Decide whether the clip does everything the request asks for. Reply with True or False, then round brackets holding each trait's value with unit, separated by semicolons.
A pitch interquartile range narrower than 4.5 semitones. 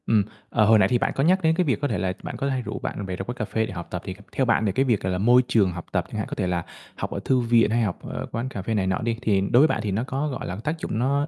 False (5.1 semitones)